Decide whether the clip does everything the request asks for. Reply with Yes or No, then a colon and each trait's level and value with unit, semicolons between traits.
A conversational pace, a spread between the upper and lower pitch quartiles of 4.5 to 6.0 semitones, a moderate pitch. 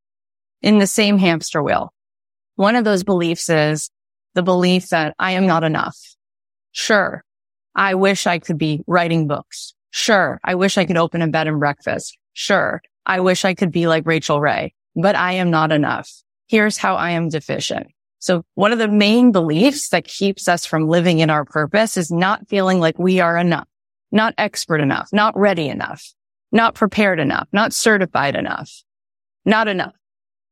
No: average, 175 wpm; average, 4.0 semitones; medium, 175 Hz